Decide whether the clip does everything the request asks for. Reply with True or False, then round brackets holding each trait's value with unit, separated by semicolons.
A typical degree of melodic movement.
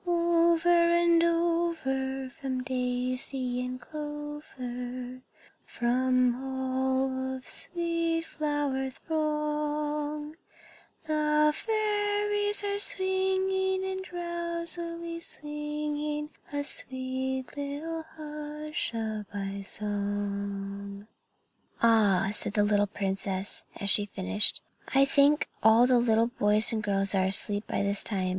False (6.1 semitones)